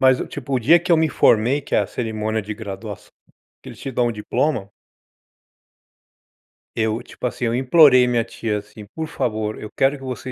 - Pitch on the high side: No, low, 120 Hz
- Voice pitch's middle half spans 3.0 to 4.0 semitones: Yes, average, 3.6 semitones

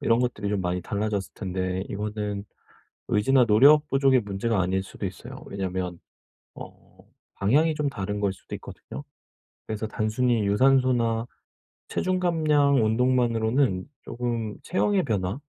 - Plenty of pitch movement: No, average, 4.6 semitones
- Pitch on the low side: Yes, low, 110 Hz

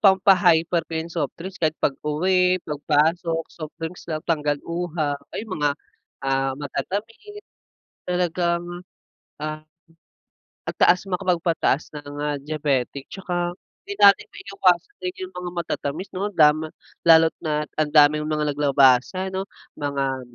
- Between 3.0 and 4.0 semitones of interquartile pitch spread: Yes, average, 3.4 semitones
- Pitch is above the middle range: No, medium, 160 Hz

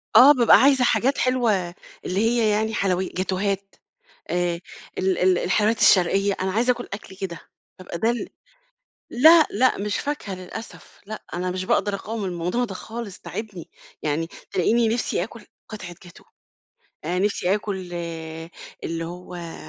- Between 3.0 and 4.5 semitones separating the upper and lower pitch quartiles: Yes, average, 4.0 semitones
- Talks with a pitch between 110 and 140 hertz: No, high, 200 Hz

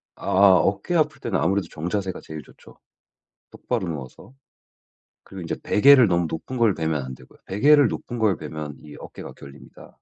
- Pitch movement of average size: No, wide, 6.9 semitones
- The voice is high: No, very low, 95 Hz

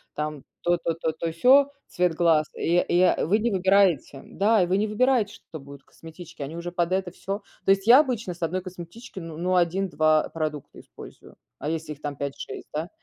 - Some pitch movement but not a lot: Yes, average, 3.6 semitones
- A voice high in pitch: No, medium, 175 Hz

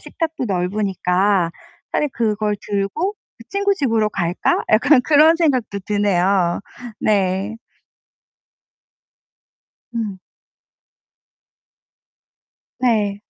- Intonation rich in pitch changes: No, average, 4.9 semitones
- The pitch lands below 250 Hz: Yes, high, 210 Hz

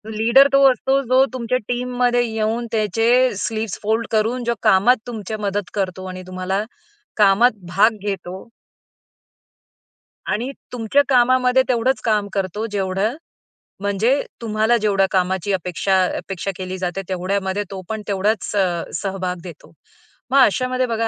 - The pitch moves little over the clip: No, average, 4.0 semitones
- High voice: Yes, high, 215 Hz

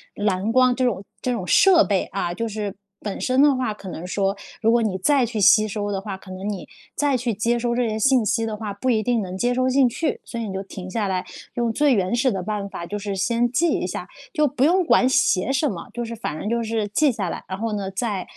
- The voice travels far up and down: No, average, 4.0 semitones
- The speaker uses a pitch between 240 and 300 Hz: No, high, 220 Hz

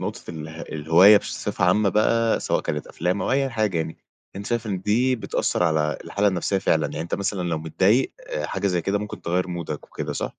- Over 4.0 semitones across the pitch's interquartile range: Yes, average, 4.5 semitones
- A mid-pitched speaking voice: No, very low, 95 Hz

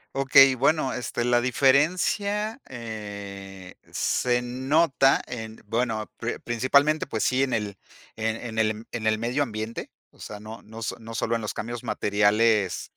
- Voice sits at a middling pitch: No, low, 115 Hz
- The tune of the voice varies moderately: Yes, average, 3.4 semitones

